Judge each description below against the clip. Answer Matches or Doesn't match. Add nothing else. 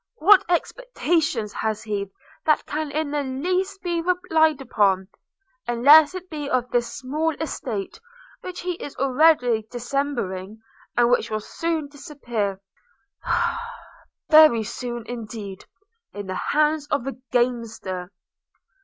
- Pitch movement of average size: Doesn't match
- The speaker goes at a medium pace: Doesn't match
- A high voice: Matches